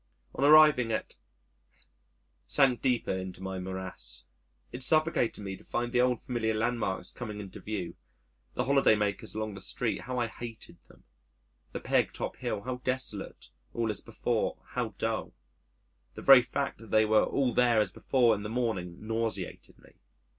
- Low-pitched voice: Yes, low, 115 Hz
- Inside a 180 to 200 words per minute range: No, average, 165 wpm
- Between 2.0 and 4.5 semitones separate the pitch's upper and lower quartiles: Yes, average, 3.5 semitones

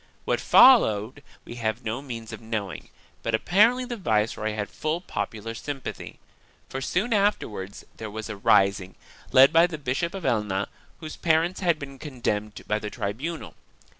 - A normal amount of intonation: No, wide, 7.4 semitones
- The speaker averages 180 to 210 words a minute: No, average, 165 wpm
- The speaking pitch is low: Yes, low, 120 Hz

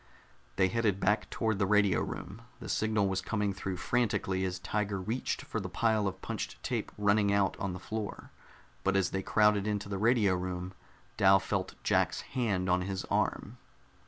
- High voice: No, low, 100 Hz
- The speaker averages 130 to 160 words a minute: No, average, 180 wpm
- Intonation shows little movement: Yes, narrow, 2.1 semitones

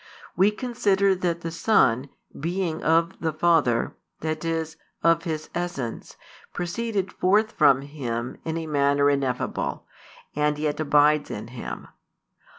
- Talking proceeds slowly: Yes, slow, 130 wpm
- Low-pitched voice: No, medium, 160 Hz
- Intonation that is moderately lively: Yes, average, 3.7 semitones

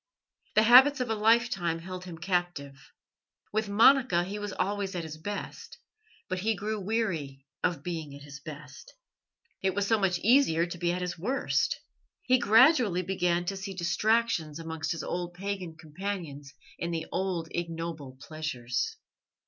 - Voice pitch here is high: No, medium, 180 Hz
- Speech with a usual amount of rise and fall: Yes, average, 4.2 semitones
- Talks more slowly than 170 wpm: Yes, average, 155 wpm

